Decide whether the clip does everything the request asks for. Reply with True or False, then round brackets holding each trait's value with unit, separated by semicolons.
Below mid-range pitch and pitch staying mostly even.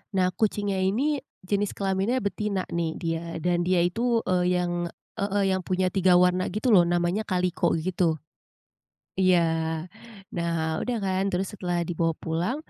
False (185 Hz; 2.2 semitones)